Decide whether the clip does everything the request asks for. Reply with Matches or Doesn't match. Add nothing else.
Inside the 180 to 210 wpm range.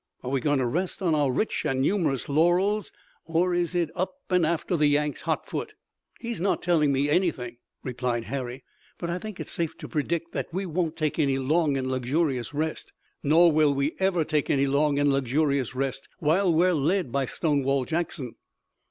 Matches